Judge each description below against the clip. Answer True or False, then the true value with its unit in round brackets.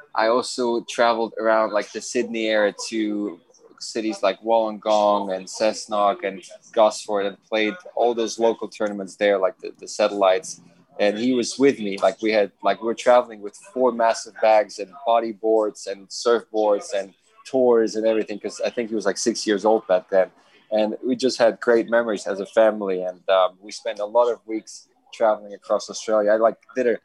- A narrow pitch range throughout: True (1.9 semitones)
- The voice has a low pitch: True (110 Hz)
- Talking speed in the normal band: True (190 wpm)